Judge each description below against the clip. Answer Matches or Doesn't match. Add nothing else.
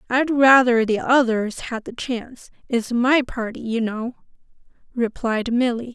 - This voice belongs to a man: Doesn't match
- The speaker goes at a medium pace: Doesn't match